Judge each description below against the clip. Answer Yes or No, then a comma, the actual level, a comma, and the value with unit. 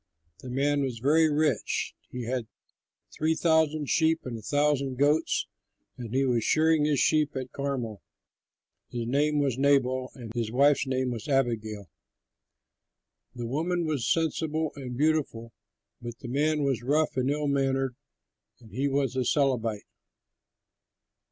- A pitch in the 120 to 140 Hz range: Yes, low, 135 Hz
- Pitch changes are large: No, average, 3.4 semitones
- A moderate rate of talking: Yes, average, 145 wpm